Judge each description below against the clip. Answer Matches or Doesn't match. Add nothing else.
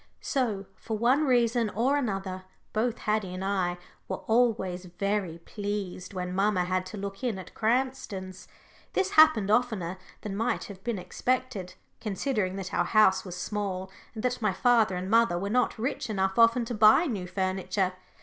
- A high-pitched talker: Matches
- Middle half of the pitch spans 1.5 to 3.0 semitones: Doesn't match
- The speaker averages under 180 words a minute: Matches